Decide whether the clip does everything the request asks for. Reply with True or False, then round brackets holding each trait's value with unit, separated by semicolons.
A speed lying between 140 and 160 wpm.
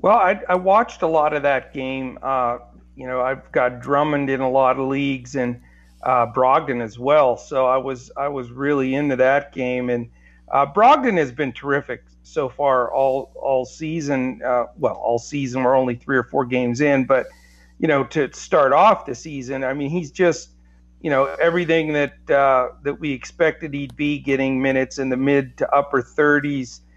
False (190 wpm)